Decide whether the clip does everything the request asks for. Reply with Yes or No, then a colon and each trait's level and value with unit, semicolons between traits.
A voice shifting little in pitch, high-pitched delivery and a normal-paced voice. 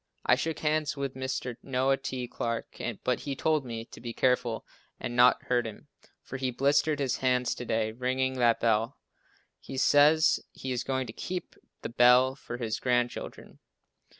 No: narrow, 2.1 semitones; low, 125 Hz; average, 175 wpm